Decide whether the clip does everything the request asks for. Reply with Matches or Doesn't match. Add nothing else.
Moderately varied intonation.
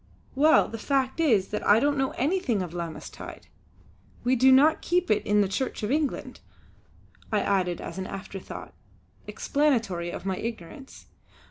Doesn't match